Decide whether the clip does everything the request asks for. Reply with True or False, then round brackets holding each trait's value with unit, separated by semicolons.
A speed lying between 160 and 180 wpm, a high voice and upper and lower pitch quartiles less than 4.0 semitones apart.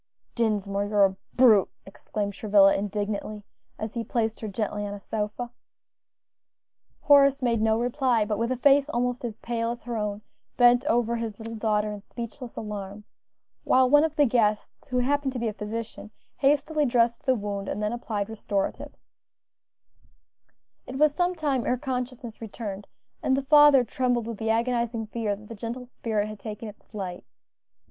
True (170 wpm; 230 Hz; 3.1 semitones)